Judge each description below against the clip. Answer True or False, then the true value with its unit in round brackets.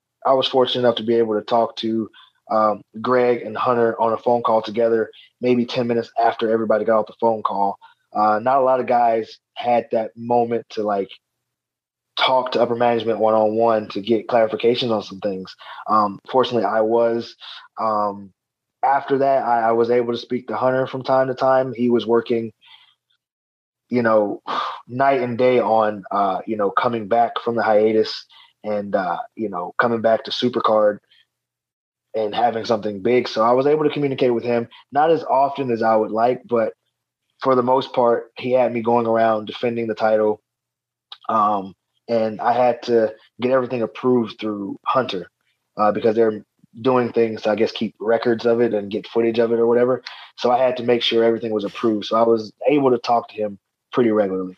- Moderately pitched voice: False (115 Hz)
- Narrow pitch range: True (2.0 semitones)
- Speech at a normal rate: True (195 wpm)